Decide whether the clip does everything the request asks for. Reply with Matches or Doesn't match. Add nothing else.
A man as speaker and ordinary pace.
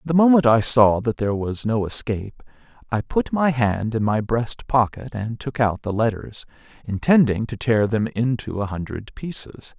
Matches